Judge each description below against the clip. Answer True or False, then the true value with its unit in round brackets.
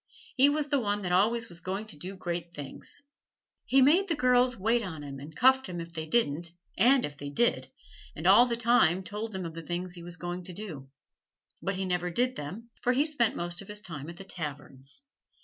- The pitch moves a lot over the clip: True (5.9 semitones)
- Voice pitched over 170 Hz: True (190 Hz)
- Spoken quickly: True (220 wpm)